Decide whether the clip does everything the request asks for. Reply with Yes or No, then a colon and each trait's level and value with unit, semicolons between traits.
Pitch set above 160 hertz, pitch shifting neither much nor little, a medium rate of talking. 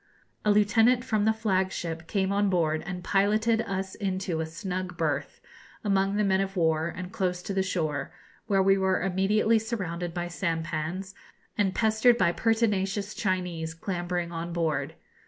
Yes: high, 190 Hz; average, 3.1 semitones; average, 160 wpm